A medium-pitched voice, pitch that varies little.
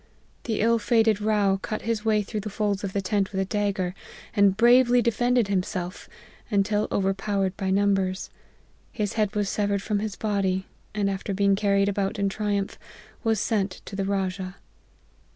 No: high, 200 Hz; narrow, 1.7 semitones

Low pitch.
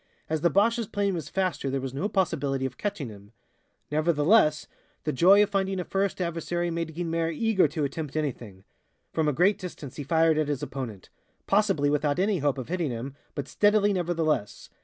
No: medium, 160 Hz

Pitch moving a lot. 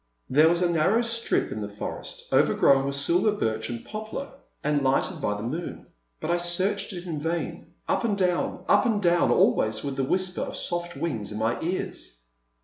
Yes: wide, 5.7 semitones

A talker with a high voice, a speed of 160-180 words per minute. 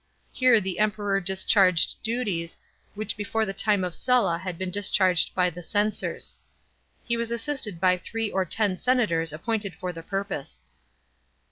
No: high, 195 Hz; average, 150 wpm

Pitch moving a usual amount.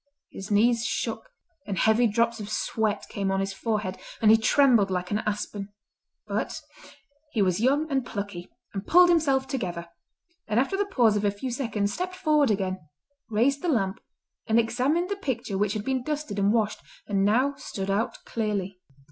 Yes: average, 4.9 semitones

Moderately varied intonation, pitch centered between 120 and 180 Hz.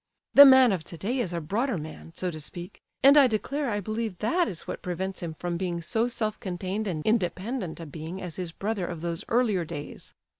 No: average, 4.8 semitones; high, 190 Hz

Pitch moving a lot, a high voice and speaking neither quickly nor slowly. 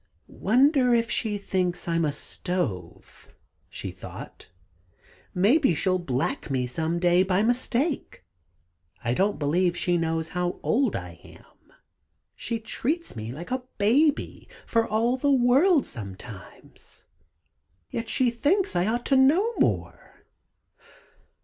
No: wide, 7.4 semitones; high, 200 Hz; slow, 125 wpm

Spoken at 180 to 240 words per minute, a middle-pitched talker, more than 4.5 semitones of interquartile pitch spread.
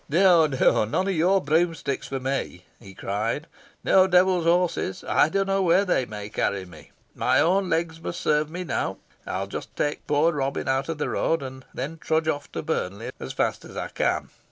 Yes: average, 200 wpm; medium, 155 Hz; average, 4.9 semitones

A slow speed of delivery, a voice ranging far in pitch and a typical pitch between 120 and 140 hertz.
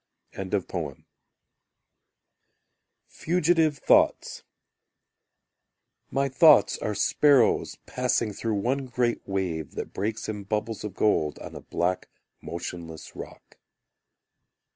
No: slow, 90 wpm; wide, 5.9 semitones; low, 110 Hz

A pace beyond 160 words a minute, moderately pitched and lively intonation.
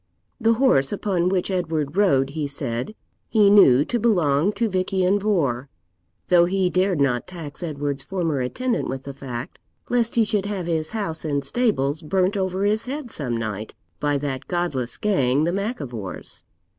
Yes: average, 170 wpm; medium, 175 Hz; wide, 6.5 semitones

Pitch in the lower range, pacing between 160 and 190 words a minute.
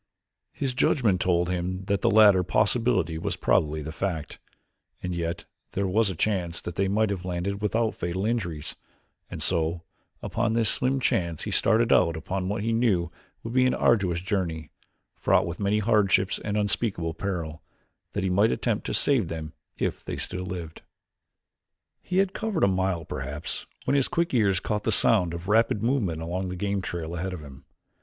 Yes: very low, 95 Hz; average, 180 wpm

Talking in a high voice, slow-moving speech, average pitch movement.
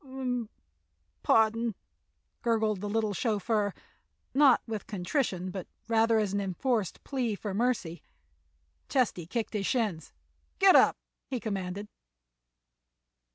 Yes: high, 220 Hz; slow, 115 wpm; average, 3.2 semitones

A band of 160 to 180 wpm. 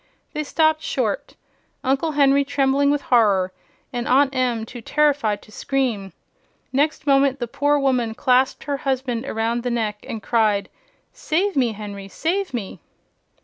No: average, 145 wpm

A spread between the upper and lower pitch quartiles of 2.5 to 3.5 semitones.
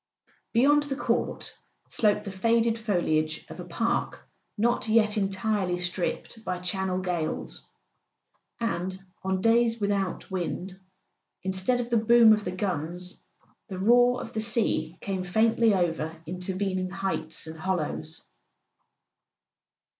No: average, 3.9 semitones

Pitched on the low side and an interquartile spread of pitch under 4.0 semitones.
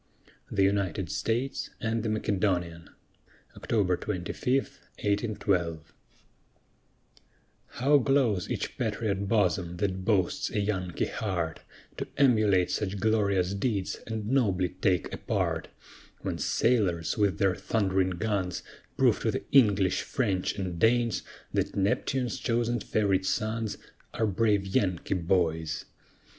Yes: low, 100 Hz; average, 3.3 semitones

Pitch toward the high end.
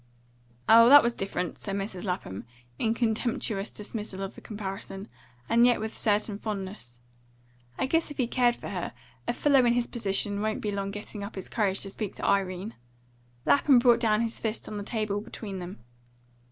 Yes: high, 210 Hz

